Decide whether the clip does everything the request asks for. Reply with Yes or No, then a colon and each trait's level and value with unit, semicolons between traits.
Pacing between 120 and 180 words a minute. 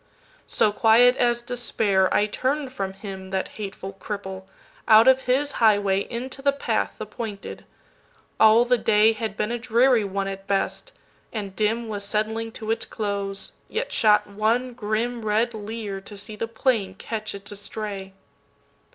Yes: average, 145 wpm